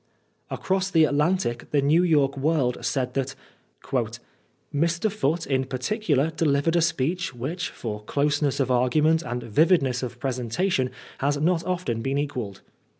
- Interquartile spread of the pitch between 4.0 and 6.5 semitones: Yes, average, 4.4 semitones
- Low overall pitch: No, medium, 145 Hz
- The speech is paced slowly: No, average, 150 wpm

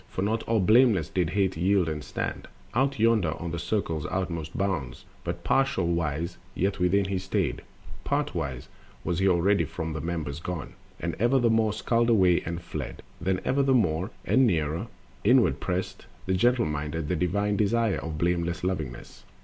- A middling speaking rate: Yes, average, 170 wpm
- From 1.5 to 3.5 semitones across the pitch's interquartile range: No, average, 4.4 semitones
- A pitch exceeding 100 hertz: No, very low, 90 Hz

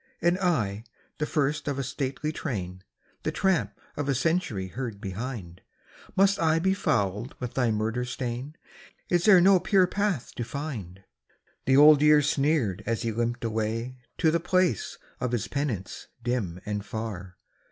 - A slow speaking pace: No, average, 165 wpm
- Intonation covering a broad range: Yes, wide, 6.3 semitones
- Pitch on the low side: Yes, low, 130 Hz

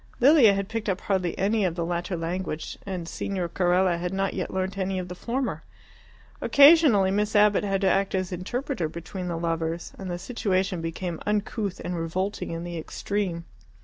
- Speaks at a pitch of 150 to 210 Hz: Yes, high, 190 Hz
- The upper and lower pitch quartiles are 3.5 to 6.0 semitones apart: No, average, 2.8 semitones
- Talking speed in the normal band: Yes, average, 180 wpm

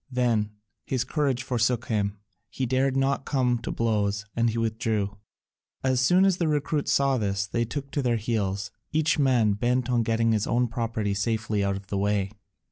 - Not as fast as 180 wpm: No, average, 185 wpm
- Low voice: Yes, low, 115 Hz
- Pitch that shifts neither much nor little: Yes, average, 3.8 semitones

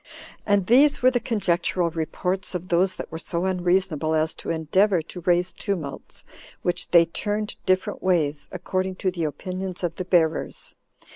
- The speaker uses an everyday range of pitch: No, narrow, 2.2 semitones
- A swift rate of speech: No, average, 160 wpm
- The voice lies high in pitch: No, medium, 180 Hz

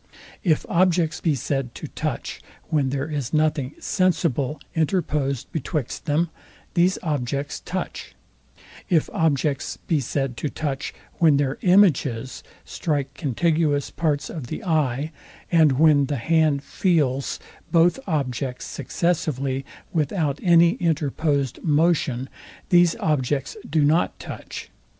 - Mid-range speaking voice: Yes, medium, 150 Hz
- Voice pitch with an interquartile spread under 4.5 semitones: Yes, average, 3.2 semitones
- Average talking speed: No, slow, 120 wpm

